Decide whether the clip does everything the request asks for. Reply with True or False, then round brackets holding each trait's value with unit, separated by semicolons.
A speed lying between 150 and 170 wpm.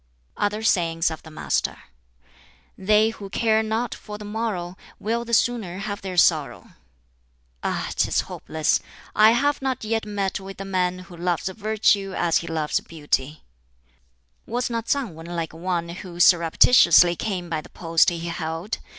True (160 wpm)